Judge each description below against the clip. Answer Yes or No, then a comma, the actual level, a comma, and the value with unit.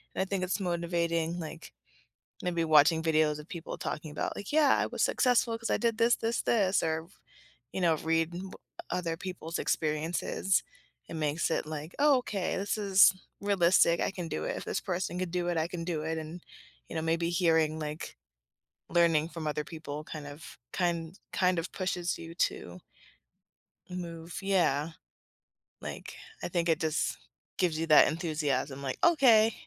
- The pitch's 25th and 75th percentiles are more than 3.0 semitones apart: No, narrow, 2.6 semitones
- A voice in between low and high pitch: Yes, medium, 170 Hz